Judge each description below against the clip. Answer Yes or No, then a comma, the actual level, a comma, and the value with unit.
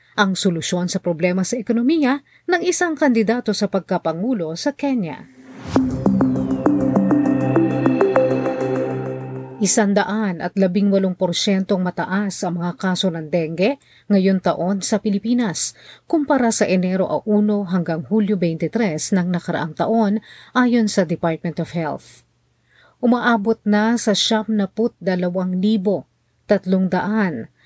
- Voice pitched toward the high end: Yes, high, 195 Hz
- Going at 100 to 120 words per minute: Yes, slow, 110 wpm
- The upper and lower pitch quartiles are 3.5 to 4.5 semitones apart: Yes, average, 4.1 semitones